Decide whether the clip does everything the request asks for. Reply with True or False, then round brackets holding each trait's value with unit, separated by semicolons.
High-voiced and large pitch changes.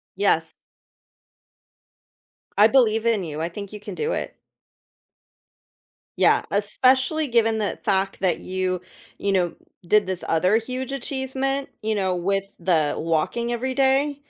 True (215 Hz; 5.8 semitones)